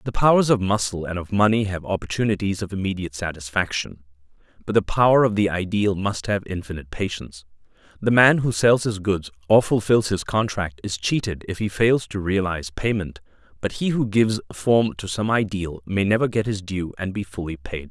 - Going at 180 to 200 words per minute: Yes, average, 190 wpm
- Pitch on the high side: No, low, 100 Hz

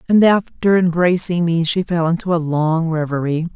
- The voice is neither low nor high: Yes, medium, 170 Hz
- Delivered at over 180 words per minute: No, average, 170 wpm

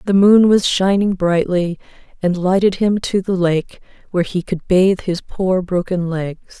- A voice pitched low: No, medium, 185 Hz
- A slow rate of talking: No, average, 175 wpm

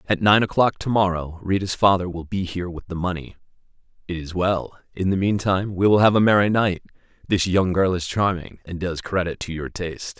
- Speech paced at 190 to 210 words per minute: Yes, fast, 205 wpm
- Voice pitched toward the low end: Yes, very low, 90 Hz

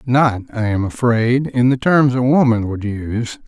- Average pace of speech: Yes, average, 190 wpm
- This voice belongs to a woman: No, male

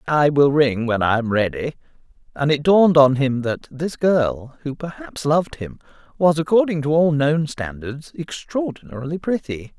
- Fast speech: No, average, 165 wpm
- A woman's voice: No, male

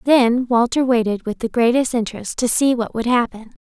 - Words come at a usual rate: Yes, average, 195 wpm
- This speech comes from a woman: Yes, female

